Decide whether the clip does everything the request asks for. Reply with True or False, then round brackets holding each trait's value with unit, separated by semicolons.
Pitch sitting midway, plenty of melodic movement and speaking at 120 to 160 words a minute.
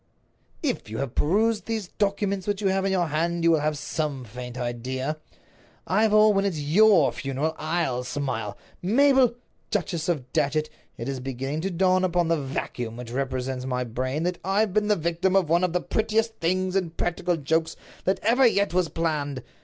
False (165 Hz; 6.2 semitones; 185 wpm)